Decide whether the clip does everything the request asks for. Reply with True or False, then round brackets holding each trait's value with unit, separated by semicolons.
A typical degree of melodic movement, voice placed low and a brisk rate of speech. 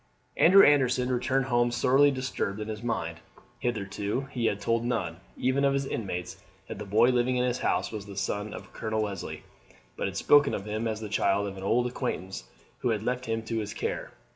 True (3.6 semitones; 115 Hz; 210 wpm)